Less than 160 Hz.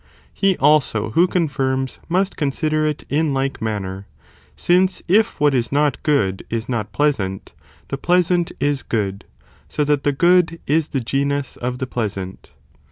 Yes: medium, 140 Hz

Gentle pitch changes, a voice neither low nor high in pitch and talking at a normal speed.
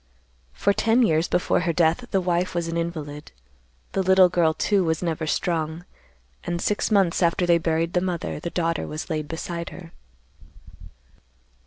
Yes: narrow, 1.9 semitones; medium, 170 Hz; average, 165 wpm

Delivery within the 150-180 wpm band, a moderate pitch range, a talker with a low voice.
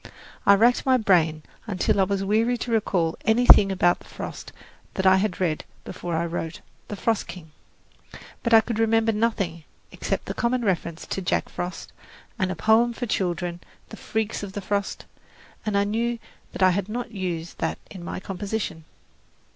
No: average, 175 wpm; average, 3.9 semitones; high, 200 Hz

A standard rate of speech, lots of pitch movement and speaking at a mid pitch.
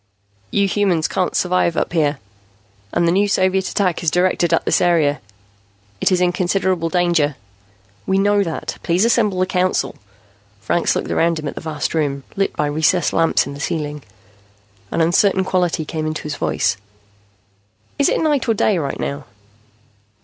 No: average, 170 wpm; average, 3.3 semitones; medium, 175 Hz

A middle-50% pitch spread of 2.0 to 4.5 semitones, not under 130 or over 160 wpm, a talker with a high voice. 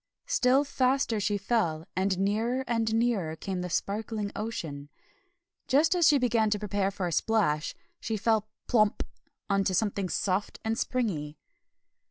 Yes: average, 3.6 semitones; average, 150 wpm; high, 210 Hz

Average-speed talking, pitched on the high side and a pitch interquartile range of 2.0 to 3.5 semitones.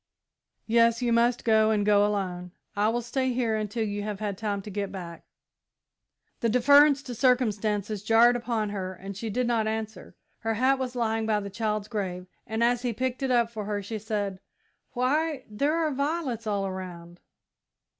Yes: average, 185 wpm; high, 220 Hz; average, 3.0 semitones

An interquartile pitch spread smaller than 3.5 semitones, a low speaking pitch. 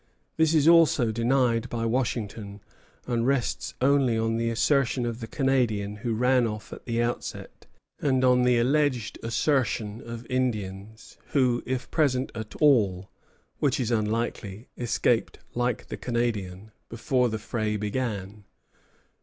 Yes: average, 2.8 semitones; low, 120 Hz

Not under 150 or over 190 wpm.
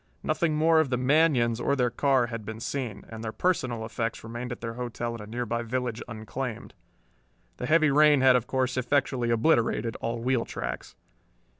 Yes: average, 180 wpm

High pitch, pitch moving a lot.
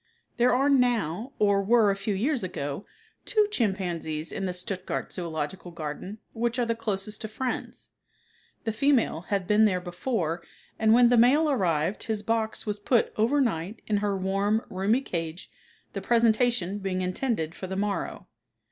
No: high, 205 Hz; average, 4.2 semitones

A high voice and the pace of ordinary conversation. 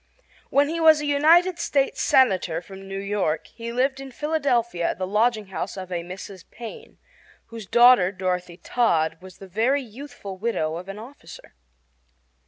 Yes: high, 215 Hz; average, 160 wpm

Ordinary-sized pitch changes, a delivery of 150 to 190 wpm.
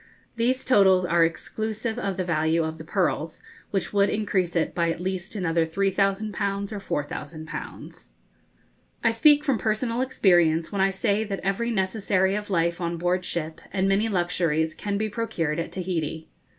Yes: average, 3.8 semitones; average, 165 wpm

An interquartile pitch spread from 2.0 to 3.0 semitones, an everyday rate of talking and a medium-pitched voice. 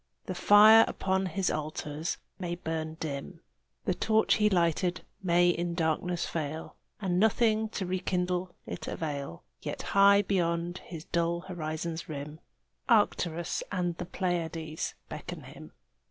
No: average, 2.7 semitones; slow, 130 wpm; medium, 175 Hz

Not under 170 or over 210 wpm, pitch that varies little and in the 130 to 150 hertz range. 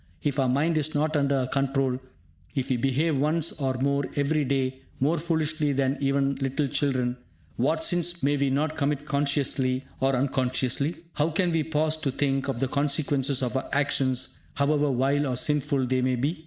Yes: average, 180 wpm; narrow, 2.2 semitones; medium, 140 Hz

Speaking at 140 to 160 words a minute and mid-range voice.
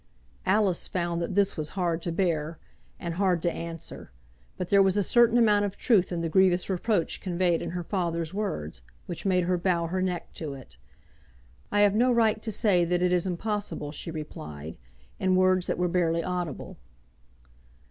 No: average, 185 wpm; medium, 180 Hz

